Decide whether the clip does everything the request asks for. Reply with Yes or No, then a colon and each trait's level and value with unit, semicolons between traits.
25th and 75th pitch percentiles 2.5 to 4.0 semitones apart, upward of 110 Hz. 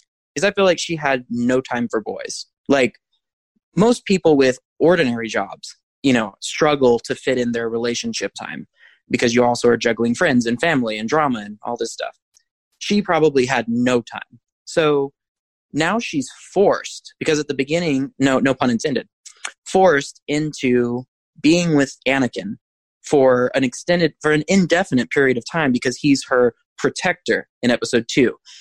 No: average, 5.0 semitones; low, 135 Hz